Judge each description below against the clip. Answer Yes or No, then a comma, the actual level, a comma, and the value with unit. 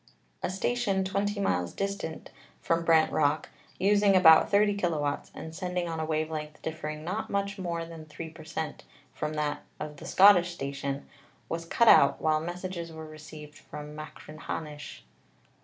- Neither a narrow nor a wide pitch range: Yes, average, 3.4 semitones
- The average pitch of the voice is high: No, medium, 160 Hz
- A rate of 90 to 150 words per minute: No, average, 160 wpm